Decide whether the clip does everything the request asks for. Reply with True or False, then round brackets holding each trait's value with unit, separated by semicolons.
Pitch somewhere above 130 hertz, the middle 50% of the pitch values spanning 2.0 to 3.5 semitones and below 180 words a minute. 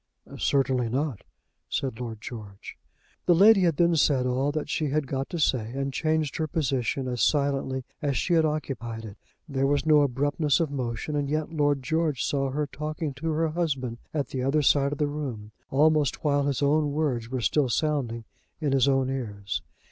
False (140 Hz; 3.1 semitones; 190 wpm)